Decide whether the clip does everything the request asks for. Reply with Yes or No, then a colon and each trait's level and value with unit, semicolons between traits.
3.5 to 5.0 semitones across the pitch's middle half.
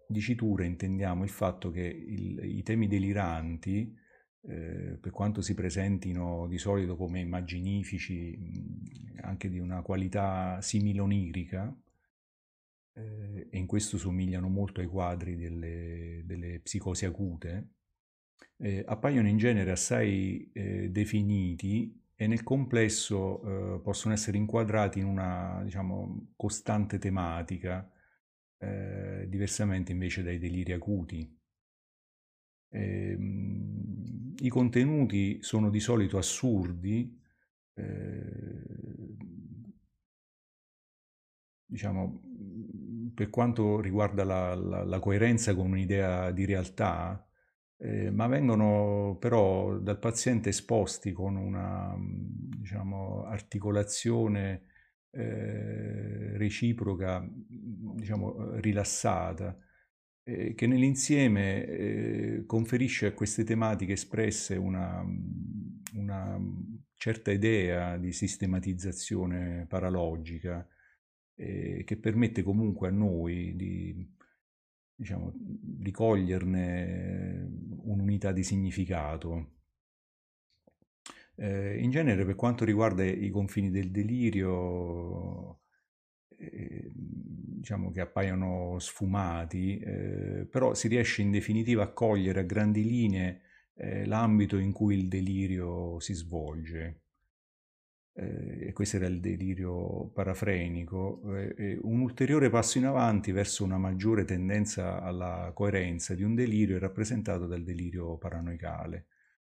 No: average, 2.7 semitones